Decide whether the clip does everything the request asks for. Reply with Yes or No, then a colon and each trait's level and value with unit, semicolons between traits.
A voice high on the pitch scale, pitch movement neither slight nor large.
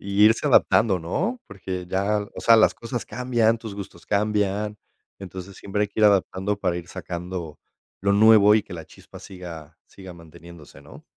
No: low, 100 Hz; average, 3.2 semitones